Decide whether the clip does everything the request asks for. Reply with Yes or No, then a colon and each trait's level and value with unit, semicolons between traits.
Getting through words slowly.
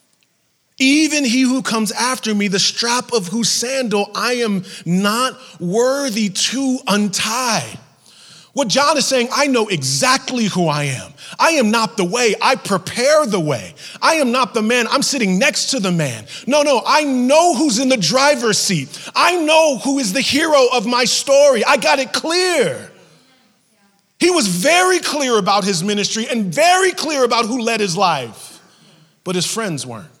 No: average, 175 wpm